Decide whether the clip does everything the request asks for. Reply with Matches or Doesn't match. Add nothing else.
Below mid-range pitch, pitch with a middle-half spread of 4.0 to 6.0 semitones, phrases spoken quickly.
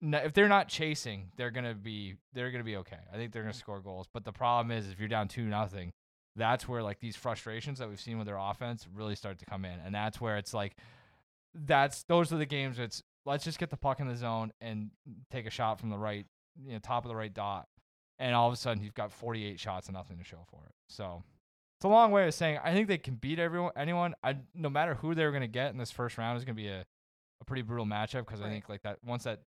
Matches